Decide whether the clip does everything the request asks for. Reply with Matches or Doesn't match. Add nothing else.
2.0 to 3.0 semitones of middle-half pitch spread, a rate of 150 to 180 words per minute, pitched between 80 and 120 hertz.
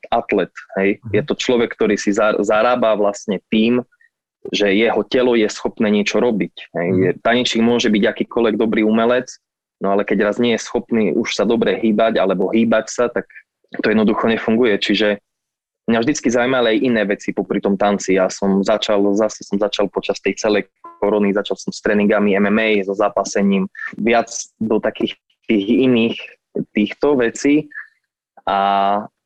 Matches